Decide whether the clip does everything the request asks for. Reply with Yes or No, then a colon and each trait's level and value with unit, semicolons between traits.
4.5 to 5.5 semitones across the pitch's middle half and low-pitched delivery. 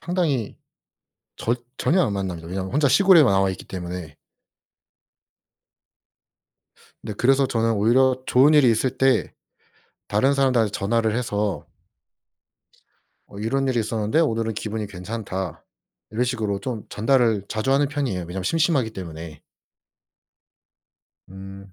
Yes: average, 5.2 semitones; low, 115 Hz